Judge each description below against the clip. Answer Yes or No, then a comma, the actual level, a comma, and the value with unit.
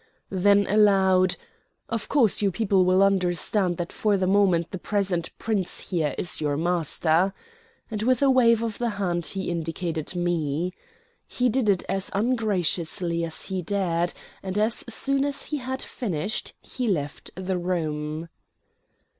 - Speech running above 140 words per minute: Yes, average, 150 wpm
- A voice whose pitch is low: No, high, 190 Hz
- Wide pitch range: No, average, 3.7 semitones